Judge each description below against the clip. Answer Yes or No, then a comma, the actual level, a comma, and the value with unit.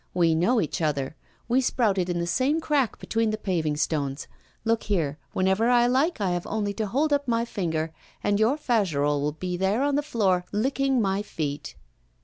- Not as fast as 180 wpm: No, average, 190 wpm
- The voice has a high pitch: Yes, high, 205 Hz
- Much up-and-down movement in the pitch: Yes, wide, 6.3 semitones